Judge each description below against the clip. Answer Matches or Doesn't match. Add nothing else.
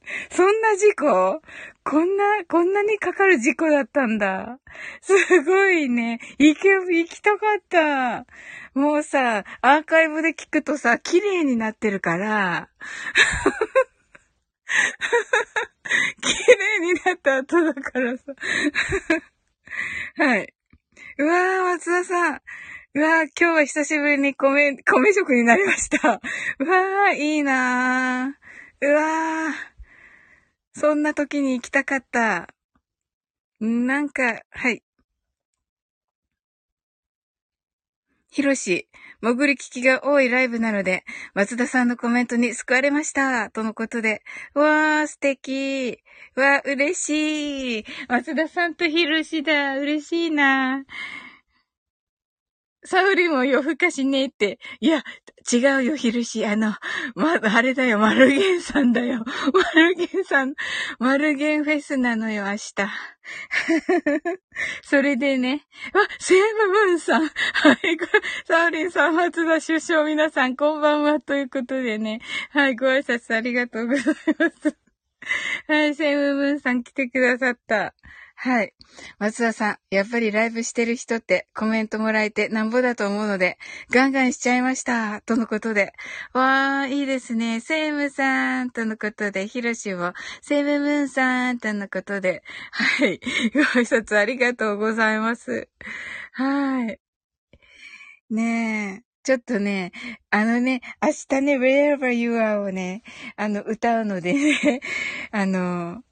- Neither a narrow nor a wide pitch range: Matches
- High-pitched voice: Matches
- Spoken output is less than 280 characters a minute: Matches